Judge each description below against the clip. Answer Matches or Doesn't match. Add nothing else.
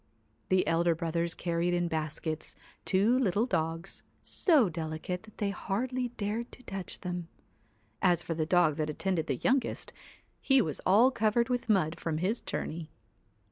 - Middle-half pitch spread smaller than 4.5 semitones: Doesn't match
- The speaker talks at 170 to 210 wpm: Matches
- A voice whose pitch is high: Doesn't match